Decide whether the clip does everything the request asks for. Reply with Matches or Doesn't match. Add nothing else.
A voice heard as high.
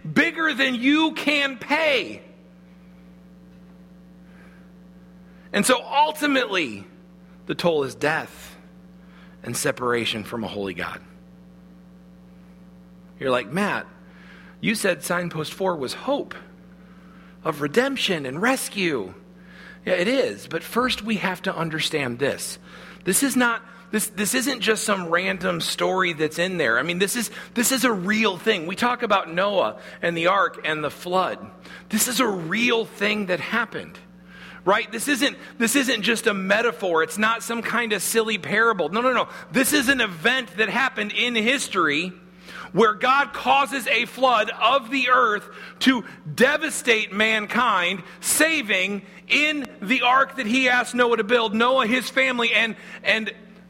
Matches